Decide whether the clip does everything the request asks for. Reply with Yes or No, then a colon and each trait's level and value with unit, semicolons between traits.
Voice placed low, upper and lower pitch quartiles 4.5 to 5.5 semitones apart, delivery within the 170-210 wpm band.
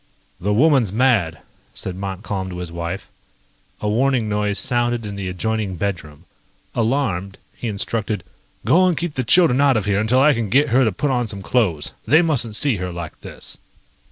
Yes: low, 110 Hz; average, 5.2 semitones; average, 185 wpm